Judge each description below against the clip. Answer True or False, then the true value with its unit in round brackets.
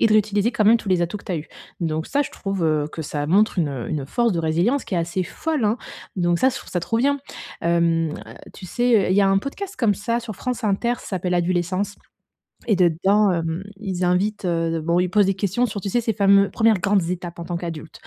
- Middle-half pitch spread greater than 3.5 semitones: True (4.1 semitones)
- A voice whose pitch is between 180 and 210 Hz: True (190 Hz)